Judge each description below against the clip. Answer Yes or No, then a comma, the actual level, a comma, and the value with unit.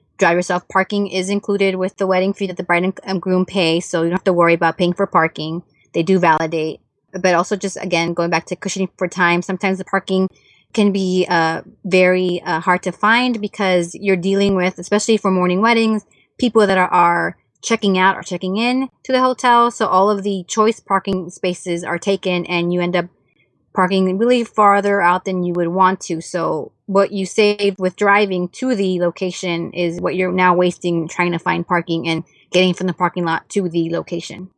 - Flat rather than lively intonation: Yes, narrow, 2.1 semitones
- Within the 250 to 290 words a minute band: No, fast, 205 wpm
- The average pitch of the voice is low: No, medium, 185 Hz